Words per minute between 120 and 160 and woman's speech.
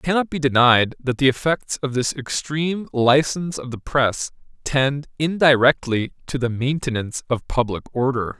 No: average, 155 wpm; male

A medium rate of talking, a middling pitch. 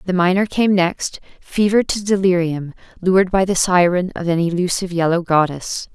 Yes: average, 160 wpm; medium, 180 Hz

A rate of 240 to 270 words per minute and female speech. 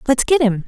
Yes: fast, 265 wpm; female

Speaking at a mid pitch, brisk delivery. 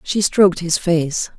No: medium, 175 Hz; average, 175 wpm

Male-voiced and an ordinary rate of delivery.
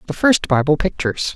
Yes: male; average, 175 wpm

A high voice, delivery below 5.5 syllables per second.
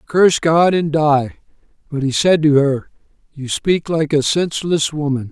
No: medium, 150 Hz; 4.5 syllables/s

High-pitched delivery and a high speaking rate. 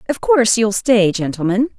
No: high, 225 Hz; average, 170 wpm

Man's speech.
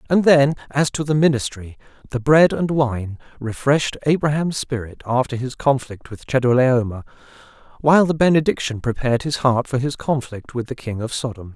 Yes: male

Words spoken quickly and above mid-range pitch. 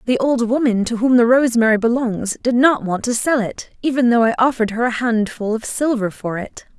Yes: fast, 220 wpm; high, 235 Hz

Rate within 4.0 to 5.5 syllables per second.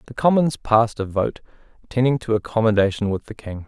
No: 5.9 syllables/s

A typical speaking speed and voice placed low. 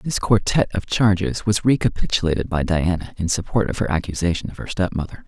Yes: average, 180 wpm; very low, 95 Hz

